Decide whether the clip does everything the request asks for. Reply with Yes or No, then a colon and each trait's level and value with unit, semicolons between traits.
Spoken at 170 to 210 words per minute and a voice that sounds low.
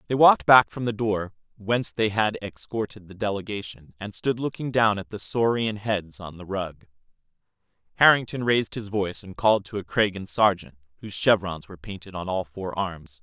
Yes: average, 185 wpm; low, 100 Hz